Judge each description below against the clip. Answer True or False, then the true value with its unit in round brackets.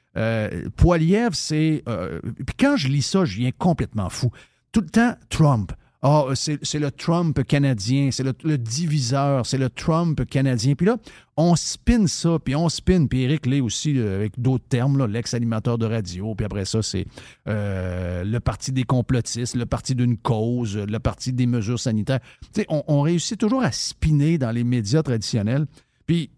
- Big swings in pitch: False (4.7 semitones)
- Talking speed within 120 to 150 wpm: False (180 wpm)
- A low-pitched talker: True (130 Hz)